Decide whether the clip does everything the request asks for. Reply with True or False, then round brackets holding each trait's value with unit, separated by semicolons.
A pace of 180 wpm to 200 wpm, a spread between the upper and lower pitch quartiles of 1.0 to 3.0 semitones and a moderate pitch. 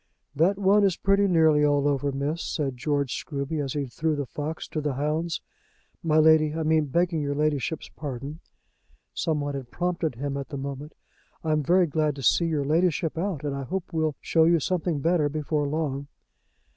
True (190 wpm; 2.5 semitones; 150 Hz)